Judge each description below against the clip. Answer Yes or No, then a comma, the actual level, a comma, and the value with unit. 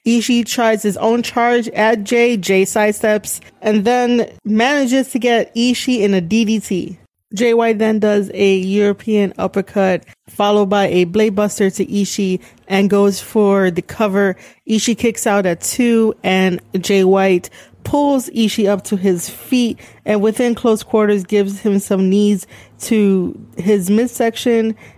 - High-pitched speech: Yes, high, 210 Hz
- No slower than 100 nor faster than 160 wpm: Yes, average, 145 wpm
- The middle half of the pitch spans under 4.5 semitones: Yes, average, 2.8 semitones